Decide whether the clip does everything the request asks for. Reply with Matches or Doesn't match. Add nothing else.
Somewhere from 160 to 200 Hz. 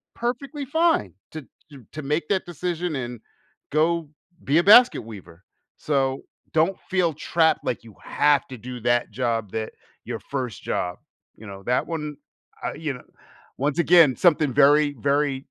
Doesn't match